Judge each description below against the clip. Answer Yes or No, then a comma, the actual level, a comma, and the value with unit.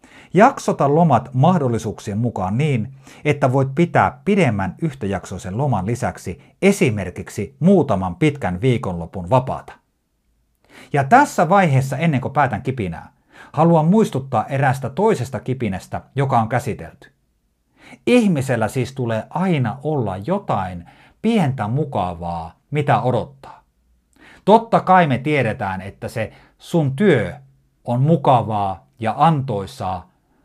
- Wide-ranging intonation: Yes, wide, 7.4 semitones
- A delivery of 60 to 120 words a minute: Yes, average, 105 wpm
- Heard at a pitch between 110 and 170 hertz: Yes, low, 125 Hz